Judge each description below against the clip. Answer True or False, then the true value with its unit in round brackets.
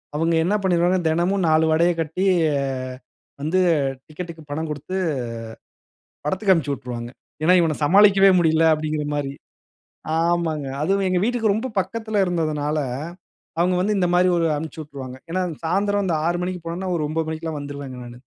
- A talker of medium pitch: True (165 Hz)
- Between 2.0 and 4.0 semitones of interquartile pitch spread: True (3.3 semitones)